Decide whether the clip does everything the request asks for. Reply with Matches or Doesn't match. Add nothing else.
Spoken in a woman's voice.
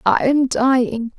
Matches